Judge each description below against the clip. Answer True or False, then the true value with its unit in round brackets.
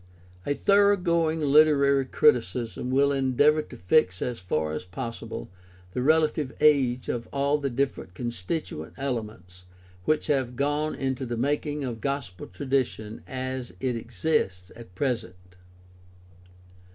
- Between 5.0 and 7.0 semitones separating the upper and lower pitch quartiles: False (4.2 semitones)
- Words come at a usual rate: False (125 wpm)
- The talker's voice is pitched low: True (130 Hz)